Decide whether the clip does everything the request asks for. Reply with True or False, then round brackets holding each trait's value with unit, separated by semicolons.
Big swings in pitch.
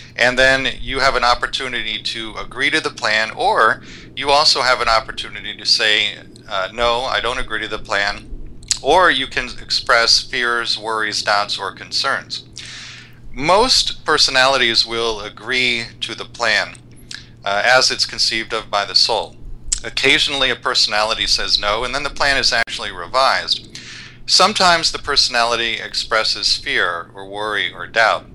False (3.0 semitones)